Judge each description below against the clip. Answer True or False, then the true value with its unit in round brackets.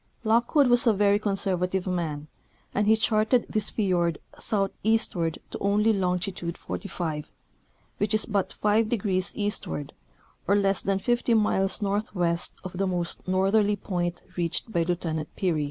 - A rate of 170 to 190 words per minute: False (145 wpm)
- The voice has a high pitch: True (195 Hz)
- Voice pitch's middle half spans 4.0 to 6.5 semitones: False (3.2 semitones)